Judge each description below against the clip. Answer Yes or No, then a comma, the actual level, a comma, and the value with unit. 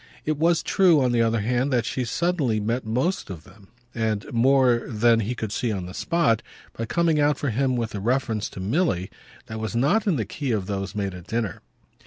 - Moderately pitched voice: No, low, 115 Hz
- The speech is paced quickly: Yes, fast, 220 wpm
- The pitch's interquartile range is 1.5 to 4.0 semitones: No, average, 4.5 semitones